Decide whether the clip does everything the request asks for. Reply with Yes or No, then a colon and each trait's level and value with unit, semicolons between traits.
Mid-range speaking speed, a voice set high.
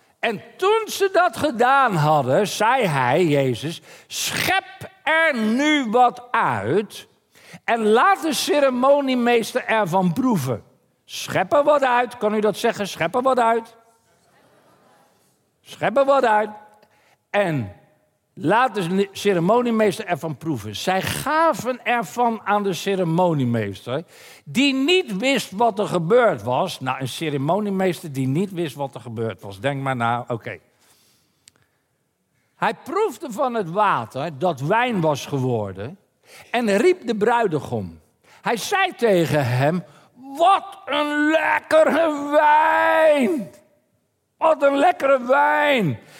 No: slow, 125 wpm; high, 215 Hz